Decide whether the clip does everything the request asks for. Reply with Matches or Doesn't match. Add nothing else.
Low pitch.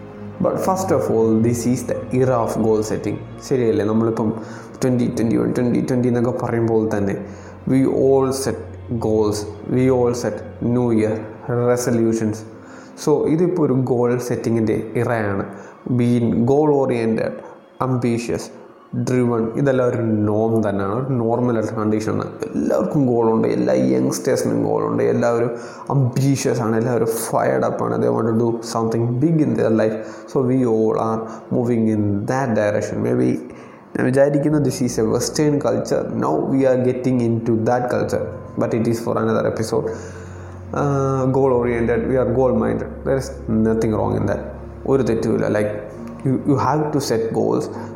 Matches